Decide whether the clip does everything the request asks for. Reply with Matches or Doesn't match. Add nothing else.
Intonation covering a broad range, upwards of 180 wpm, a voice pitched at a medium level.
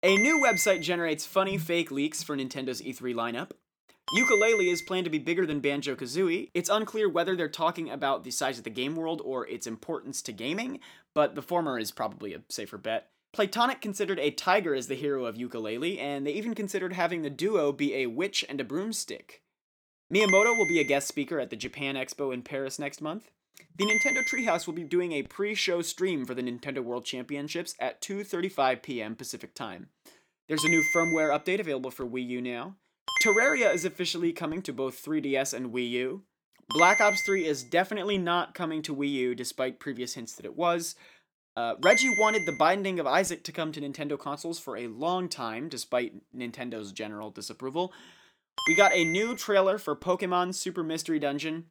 Matches